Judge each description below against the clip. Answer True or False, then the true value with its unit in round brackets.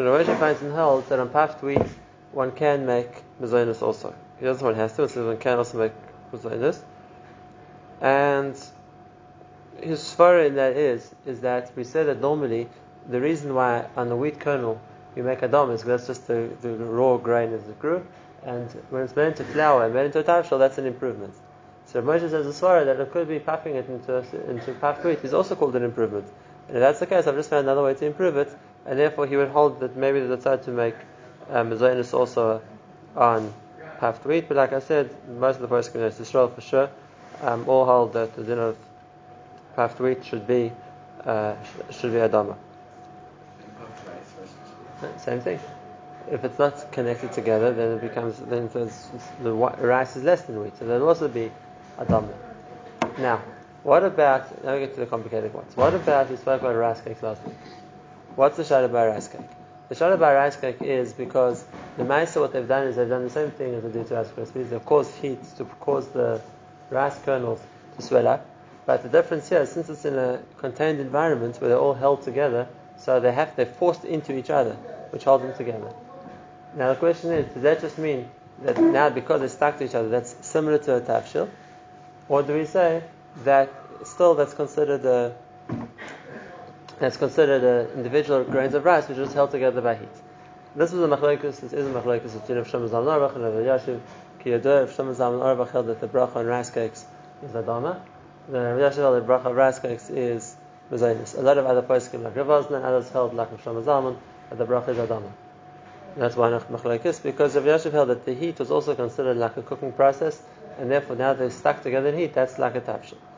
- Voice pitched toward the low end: True (130 Hz)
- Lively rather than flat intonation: False (3.3 semitones)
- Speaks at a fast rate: True (210 wpm)